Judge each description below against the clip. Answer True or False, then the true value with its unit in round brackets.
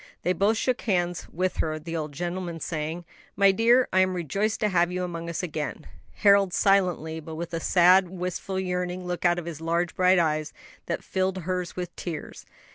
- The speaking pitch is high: False (180 Hz)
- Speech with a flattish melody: True (2.1 semitones)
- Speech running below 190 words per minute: False (195 wpm)